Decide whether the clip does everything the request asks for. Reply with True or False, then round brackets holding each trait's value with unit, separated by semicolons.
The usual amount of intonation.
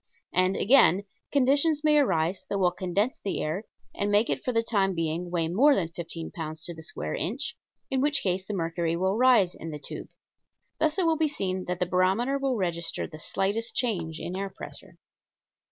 False (6.3 semitones)